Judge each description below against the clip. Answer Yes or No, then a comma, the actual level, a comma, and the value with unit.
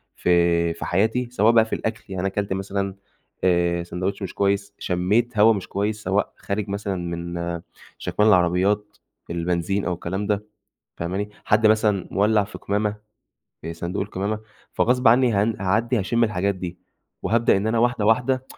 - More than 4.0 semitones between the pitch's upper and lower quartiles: No, average, 3.2 semitones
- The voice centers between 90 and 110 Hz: Yes, low, 100 Hz